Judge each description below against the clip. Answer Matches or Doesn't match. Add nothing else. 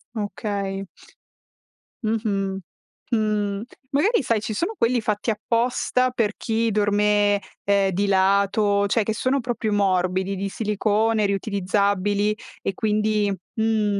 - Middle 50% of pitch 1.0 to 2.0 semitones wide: Matches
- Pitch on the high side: Matches